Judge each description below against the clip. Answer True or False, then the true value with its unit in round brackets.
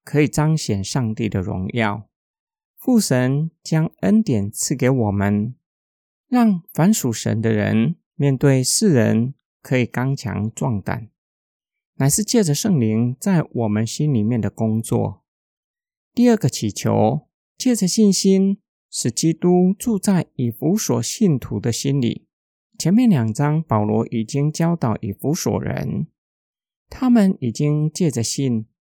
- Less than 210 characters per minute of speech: True (190 characters per minute)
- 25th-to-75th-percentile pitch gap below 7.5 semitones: False (8.1 semitones)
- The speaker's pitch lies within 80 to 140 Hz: True (135 Hz)